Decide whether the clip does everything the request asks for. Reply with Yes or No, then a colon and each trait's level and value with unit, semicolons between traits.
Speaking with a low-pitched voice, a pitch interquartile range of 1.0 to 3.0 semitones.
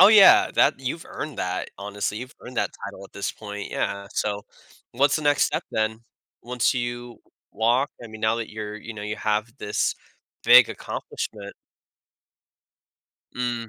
Yes: low, 110 Hz; average, 2.7 semitones